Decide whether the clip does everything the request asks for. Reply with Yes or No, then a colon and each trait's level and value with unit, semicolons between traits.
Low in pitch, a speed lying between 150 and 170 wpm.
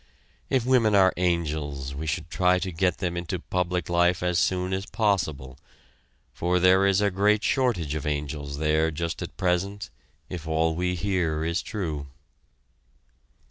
Yes: very low, 90 Hz; average, 155 wpm